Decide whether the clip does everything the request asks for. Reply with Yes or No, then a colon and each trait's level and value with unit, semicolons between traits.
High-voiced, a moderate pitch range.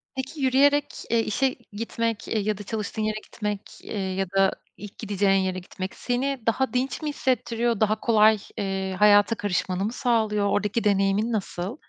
Yes: high, 215 Hz; average, 3.2 semitones